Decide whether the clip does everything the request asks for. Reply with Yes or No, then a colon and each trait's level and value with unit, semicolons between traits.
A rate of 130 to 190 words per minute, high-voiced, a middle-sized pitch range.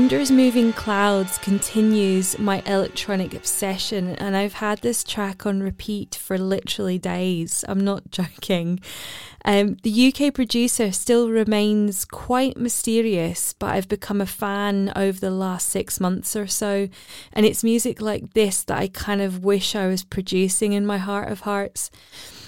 No: average, 155 wpm; high, 200 Hz; narrow, 2.1 semitones